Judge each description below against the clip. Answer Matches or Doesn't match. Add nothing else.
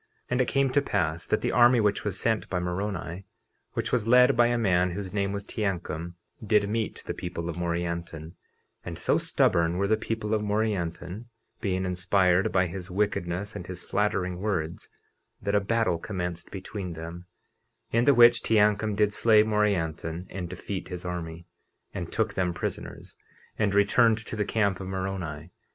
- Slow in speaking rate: Doesn't match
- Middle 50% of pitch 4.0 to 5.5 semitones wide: Doesn't match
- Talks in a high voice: Doesn't match